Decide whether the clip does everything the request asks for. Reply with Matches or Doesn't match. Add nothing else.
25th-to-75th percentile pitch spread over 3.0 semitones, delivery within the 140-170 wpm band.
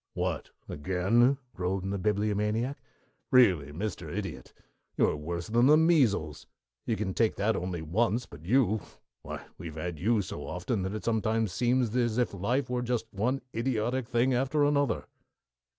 Matches